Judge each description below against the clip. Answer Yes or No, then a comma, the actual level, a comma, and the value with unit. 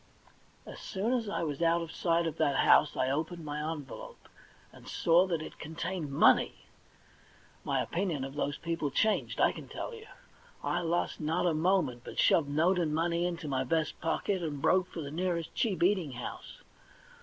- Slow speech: No, average, 185 wpm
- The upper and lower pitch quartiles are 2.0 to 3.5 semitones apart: Yes, average, 3.0 semitones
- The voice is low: No, medium, 165 Hz